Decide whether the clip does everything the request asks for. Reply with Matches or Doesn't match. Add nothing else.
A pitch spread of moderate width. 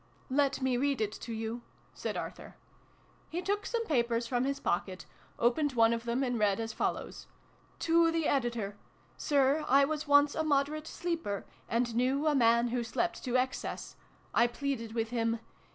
Matches